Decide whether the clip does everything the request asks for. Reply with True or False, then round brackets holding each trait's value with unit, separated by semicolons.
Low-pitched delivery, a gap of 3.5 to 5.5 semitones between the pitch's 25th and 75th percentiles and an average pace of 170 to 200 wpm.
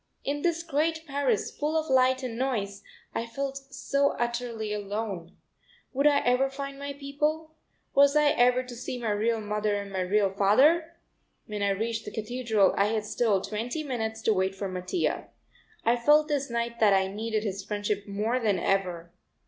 False (235 Hz; 5.2 semitones; 180 wpm)